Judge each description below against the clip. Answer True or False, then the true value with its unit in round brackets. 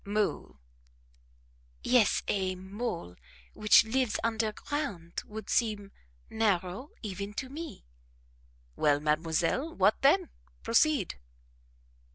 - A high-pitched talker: True (210 Hz)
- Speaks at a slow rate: True (90 wpm)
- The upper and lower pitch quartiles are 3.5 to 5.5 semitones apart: True (5.2 semitones)